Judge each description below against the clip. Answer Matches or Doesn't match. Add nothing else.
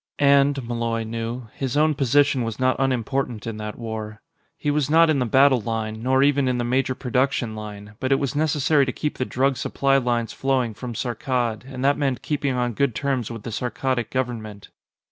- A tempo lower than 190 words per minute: Doesn't match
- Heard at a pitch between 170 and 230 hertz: Doesn't match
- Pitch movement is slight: Doesn't match